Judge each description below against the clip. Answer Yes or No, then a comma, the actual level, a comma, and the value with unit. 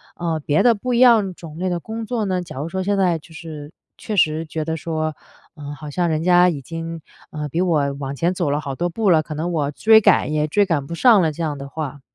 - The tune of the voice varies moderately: Yes, average, 3.4 semitones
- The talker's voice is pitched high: No, medium, 165 Hz